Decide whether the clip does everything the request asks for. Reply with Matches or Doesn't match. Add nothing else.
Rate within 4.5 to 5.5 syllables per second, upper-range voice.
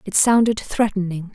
Matches